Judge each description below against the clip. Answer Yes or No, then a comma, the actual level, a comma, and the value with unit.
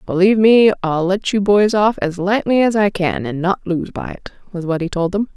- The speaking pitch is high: Yes, high, 195 Hz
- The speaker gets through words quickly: Yes, fast, 245 wpm